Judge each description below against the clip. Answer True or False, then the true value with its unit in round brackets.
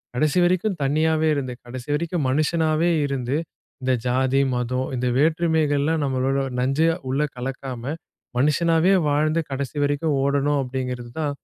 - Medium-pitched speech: True (145 Hz)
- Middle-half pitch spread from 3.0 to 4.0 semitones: True (3.3 semitones)